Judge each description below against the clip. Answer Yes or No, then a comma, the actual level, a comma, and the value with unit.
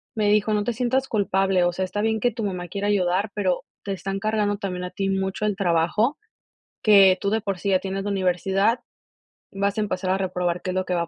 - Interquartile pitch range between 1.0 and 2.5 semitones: Yes, narrow, 2.2 semitones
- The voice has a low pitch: No, high, 195 Hz